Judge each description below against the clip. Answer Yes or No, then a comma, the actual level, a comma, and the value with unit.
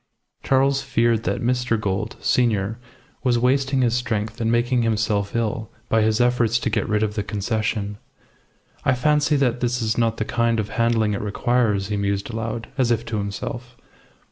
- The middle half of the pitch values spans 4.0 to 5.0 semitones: No, narrow, 2.4 semitones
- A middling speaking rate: Yes, average, 175 wpm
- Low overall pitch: Yes, low, 115 Hz